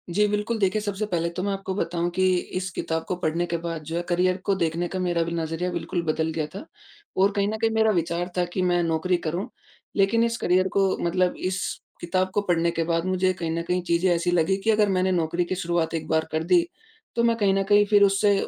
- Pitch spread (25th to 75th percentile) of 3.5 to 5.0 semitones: No, narrow, 2.6 semitones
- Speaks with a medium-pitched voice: Yes, medium, 180 Hz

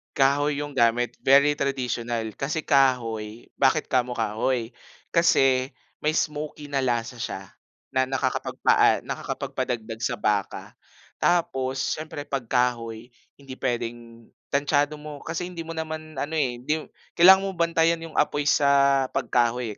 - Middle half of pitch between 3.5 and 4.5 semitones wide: Yes, average, 3.9 semitones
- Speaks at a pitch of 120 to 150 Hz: Yes, low, 135 Hz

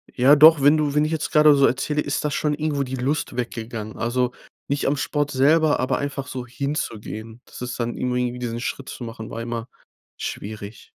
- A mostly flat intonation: No, average, 3.7 semitones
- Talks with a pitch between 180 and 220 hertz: No, low, 130 Hz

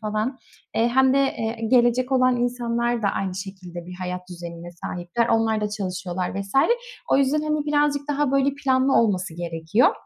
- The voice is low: No, high, 230 Hz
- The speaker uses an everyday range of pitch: No, wide, 6.1 semitones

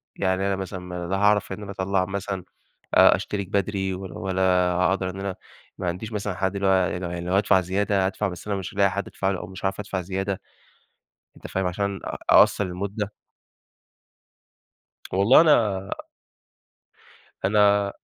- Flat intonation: Yes, narrow, 1.3 semitones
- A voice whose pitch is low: Yes, very low, 95 Hz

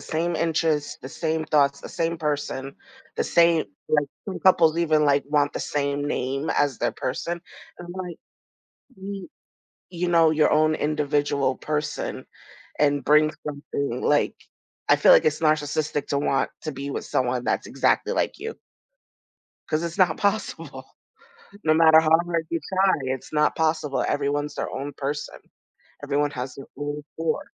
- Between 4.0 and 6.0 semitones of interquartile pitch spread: No, narrow, 2.4 semitones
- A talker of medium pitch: Yes, medium, 150 Hz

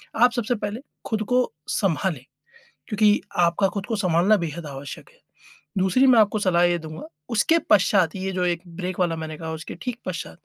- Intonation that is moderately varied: Yes, average, 4.1 semitones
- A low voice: No, medium, 185 Hz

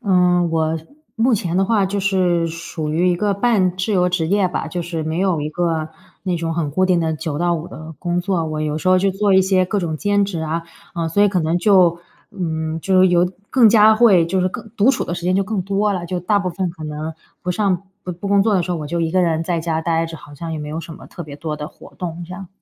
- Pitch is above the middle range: No, medium, 175 Hz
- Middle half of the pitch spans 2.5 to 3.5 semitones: Yes, average, 2.9 semitones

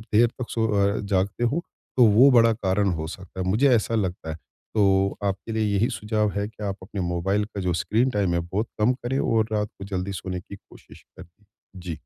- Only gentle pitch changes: No, average, 3.1 semitones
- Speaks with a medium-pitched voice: No, low, 105 Hz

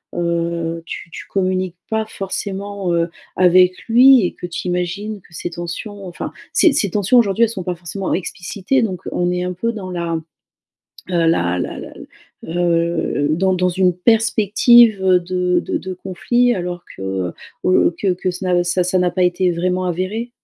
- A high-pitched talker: No, medium, 180 Hz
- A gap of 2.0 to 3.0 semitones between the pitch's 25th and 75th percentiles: Yes, narrow, 2.4 semitones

